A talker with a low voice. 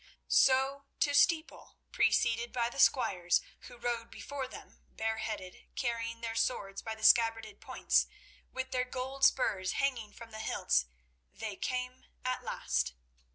No: high, 235 Hz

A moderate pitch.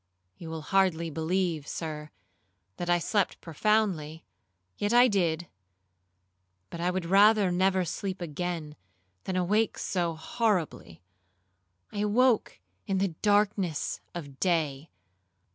Yes: medium, 180 Hz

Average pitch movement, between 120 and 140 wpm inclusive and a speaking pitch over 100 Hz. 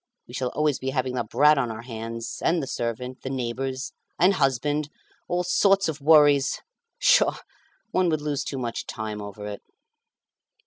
No: average, 4.1 semitones; average, 170 wpm; low, 135 Hz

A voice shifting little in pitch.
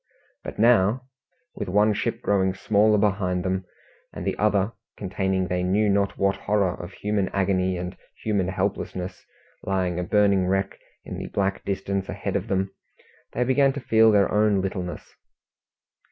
Yes: narrow, 1.9 semitones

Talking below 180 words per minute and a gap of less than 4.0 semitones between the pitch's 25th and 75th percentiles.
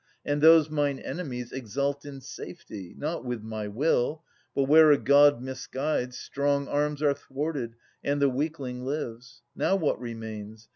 Yes: average, 160 wpm; average, 3.2 semitones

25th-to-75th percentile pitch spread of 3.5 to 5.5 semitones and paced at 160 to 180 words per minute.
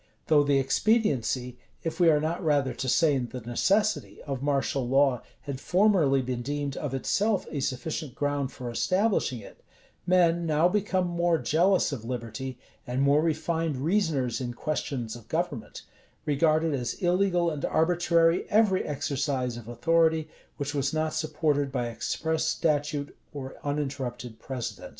No: average, 4.0 semitones; average, 150 wpm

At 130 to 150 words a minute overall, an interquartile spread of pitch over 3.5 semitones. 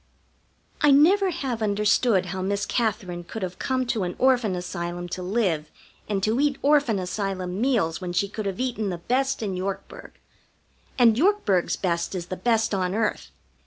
No: average, 170 wpm; average, 5.1 semitones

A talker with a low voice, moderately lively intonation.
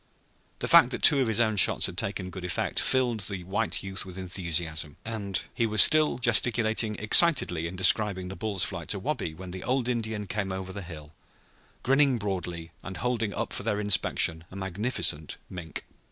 Yes: low, 100 Hz; average, 3.8 semitones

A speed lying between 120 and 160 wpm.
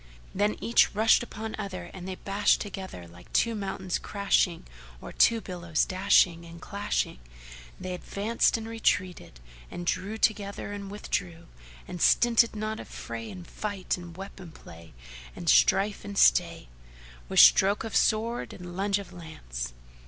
Yes: average, 150 wpm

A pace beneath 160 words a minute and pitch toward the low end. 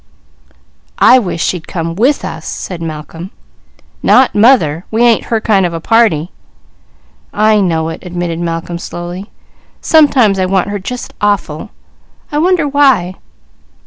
No: average, 140 wpm; high, 190 Hz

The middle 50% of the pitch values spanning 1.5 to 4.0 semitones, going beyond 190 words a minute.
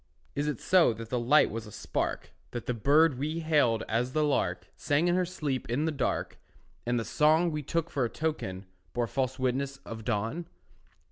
No: average, 4.8 semitones; average, 200 wpm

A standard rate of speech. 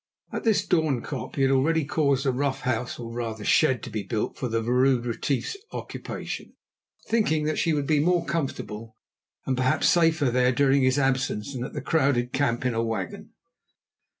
Yes: average, 180 wpm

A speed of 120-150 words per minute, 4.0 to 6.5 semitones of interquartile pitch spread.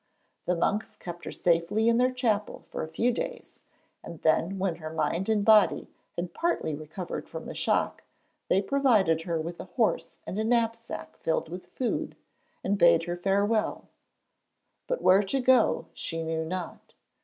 No: average, 165 wpm; average, 5.2 semitones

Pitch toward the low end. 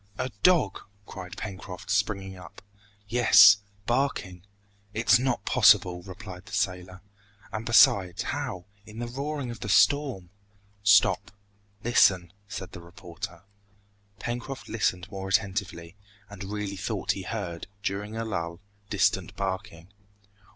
Yes: low, 100 Hz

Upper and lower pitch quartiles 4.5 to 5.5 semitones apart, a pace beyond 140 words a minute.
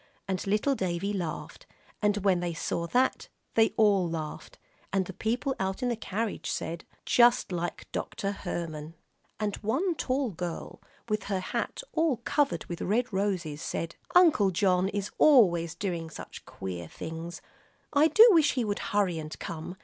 Yes: average, 5.1 semitones; average, 160 wpm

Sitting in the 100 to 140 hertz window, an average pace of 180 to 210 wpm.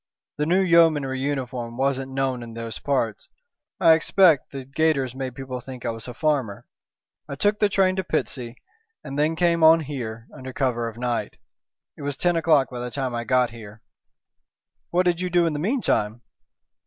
Yes: low, 135 Hz; average, 185 wpm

